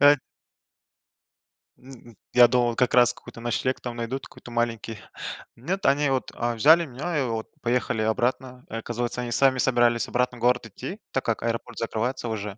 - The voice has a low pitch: Yes, low, 120 Hz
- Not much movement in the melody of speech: Yes, narrow, 1.9 semitones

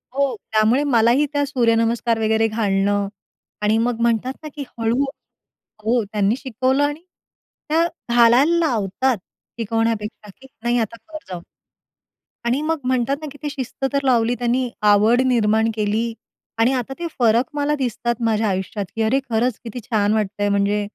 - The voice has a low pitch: No, high, 235 Hz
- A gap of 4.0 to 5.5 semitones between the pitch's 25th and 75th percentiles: No, average, 3.3 semitones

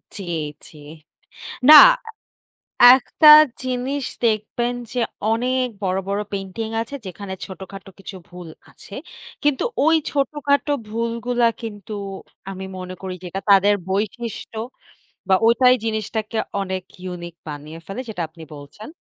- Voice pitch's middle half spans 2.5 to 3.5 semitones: No, average, 4.3 semitones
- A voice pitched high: Yes, high, 210 Hz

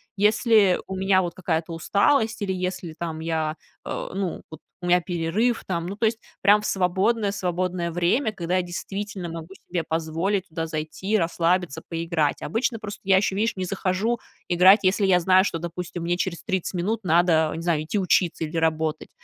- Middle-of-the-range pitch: Yes, medium, 180 Hz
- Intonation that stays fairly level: No, average, 3.1 semitones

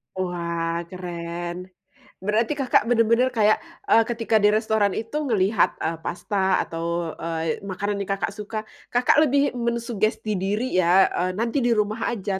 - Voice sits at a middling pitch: No, high, 205 Hz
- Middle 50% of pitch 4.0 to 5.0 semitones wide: Yes, average, 4.3 semitones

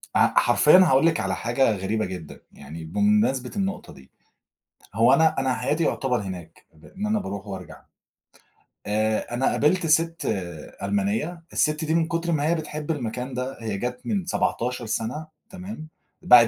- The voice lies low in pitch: Yes, low, 130 Hz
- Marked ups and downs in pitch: Yes, wide, 7.2 semitones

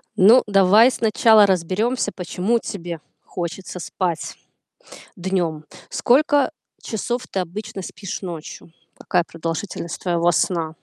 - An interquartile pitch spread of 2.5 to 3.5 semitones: No, average, 4.1 semitones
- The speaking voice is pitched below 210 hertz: Yes, high, 190 Hz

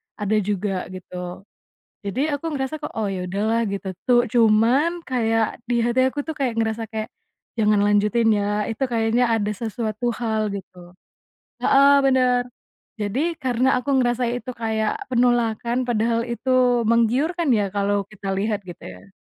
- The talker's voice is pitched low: No, high, 225 Hz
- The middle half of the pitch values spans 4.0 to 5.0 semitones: No, average, 3.2 semitones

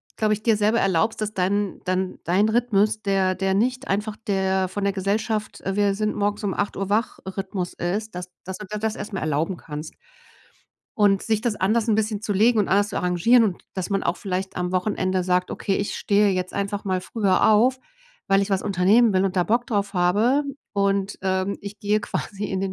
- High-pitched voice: Yes, high, 200 Hz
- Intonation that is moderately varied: No, narrow, 2.1 semitones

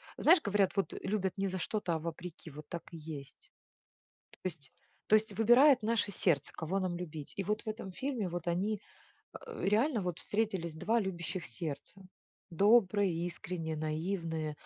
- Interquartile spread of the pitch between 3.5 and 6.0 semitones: Yes, average, 4.3 semitones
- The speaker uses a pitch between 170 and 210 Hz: Yes, medium, 185 Hz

